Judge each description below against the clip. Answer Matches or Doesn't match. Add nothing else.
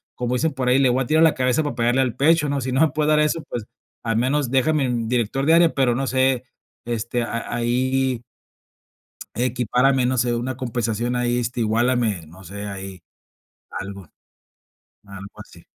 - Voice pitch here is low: Matches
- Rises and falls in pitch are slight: Matches